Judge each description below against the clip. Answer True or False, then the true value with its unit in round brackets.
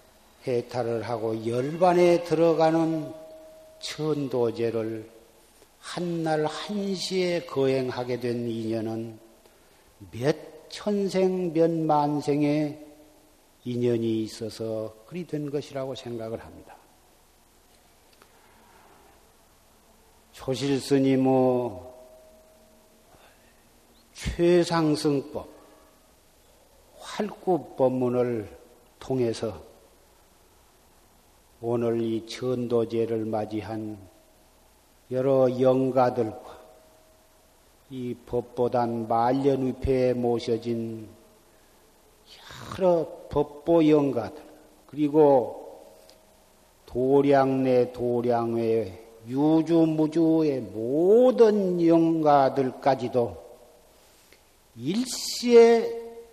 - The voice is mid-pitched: False (130 Hz)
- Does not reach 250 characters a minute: True (140 characters per minute)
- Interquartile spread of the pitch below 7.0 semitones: True (5.3 semitones)